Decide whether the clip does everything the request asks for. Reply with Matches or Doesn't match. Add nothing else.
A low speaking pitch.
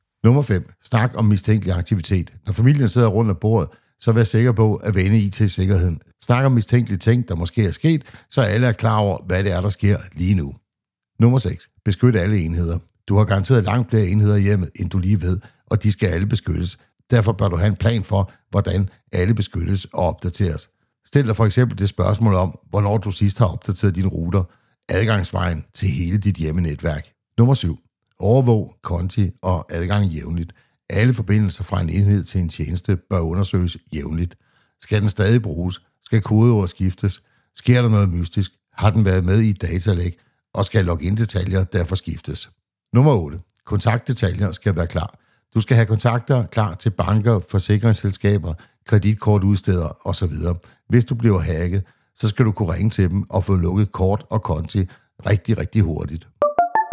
Matches